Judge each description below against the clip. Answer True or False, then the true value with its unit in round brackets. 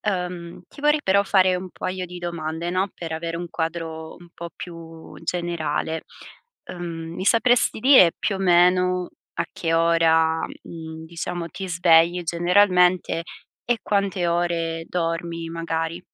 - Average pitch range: False (1.7 semitones)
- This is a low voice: False (170 Hz)